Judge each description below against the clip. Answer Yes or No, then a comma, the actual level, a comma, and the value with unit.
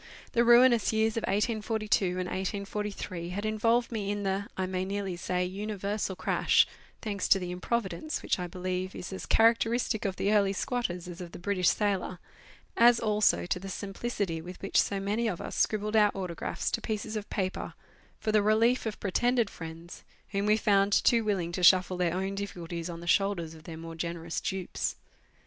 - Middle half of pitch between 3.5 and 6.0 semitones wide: No, average, 3.0 semitones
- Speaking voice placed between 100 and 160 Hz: No, high, 200 Hz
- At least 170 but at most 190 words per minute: Yes, average, 185 wpm